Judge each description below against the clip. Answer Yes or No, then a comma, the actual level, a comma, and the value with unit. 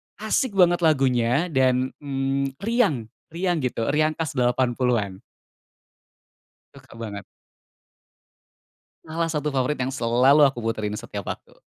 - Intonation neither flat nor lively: Yes, average, 4.5 semitones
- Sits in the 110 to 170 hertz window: Yes, low, 135 Hz